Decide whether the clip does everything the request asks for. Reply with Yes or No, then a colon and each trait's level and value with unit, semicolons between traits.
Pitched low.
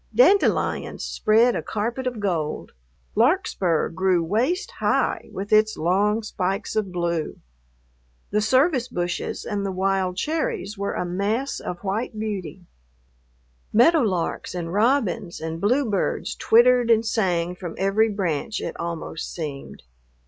No: high, 200 Hz